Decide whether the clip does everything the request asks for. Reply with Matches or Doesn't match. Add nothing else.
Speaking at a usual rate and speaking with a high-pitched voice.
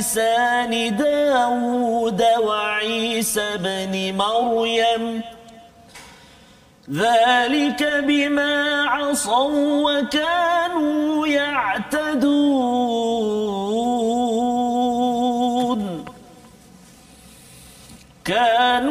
Doesn't match